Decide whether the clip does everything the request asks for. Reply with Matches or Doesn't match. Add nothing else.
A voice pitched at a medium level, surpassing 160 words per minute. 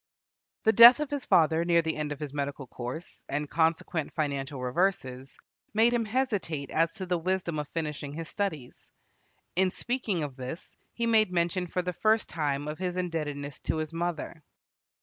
Matches